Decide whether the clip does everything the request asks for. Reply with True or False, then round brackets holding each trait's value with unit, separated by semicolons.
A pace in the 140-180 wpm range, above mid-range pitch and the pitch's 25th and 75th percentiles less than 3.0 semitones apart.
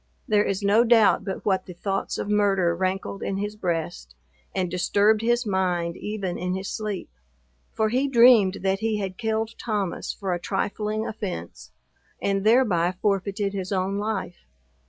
True (160 wpm; 200 Hz; 2.5 semitones)